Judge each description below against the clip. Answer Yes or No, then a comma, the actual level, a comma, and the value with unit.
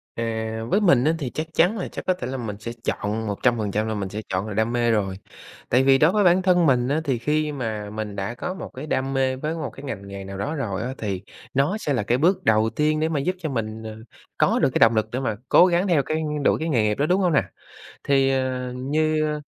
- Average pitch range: No, wide, 5.9 semitones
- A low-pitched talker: Yes, low, 130 Hz